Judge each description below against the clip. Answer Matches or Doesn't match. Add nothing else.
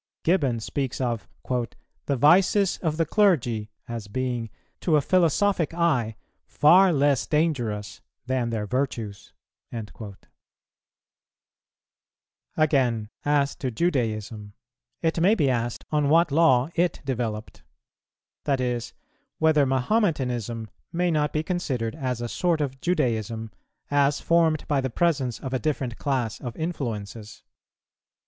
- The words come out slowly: Matches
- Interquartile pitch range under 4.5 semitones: Doesn't match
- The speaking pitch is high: Doesn't match